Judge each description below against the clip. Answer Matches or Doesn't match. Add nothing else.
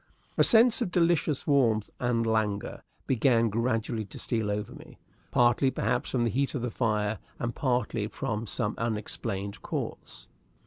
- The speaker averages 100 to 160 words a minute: Matches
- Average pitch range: Matches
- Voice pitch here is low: Matches